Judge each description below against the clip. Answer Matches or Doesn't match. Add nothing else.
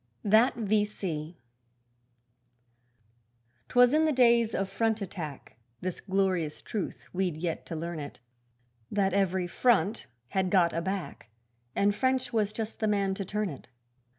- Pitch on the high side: Matches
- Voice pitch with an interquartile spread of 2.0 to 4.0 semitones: Matches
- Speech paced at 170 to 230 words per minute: Doesn't match